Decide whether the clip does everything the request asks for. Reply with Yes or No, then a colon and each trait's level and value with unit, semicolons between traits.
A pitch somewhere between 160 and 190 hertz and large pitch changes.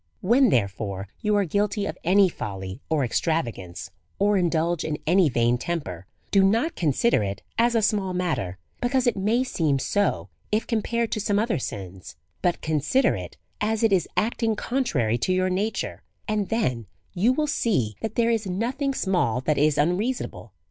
Yes: medium, 185 Hz; wide, 8.9 semitones